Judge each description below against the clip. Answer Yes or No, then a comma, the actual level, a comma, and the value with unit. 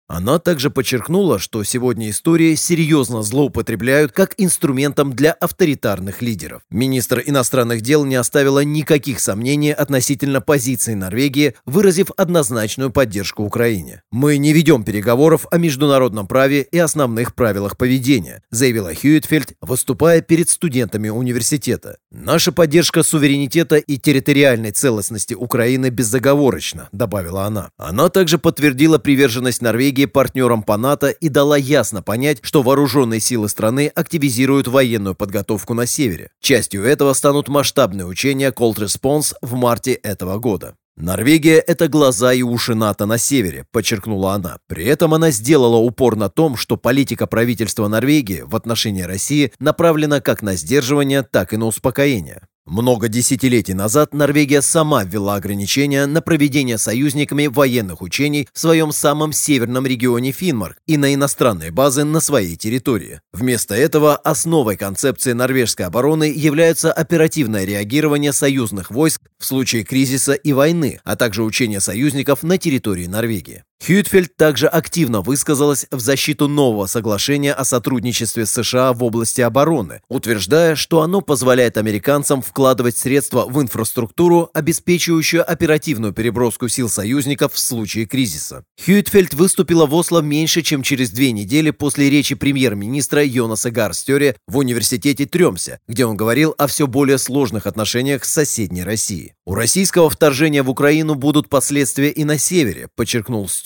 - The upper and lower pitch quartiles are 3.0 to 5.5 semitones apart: Yes, average, 4.6 semitones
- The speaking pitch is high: No, low, 135 Hz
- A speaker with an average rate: Yes, average, 140 wpm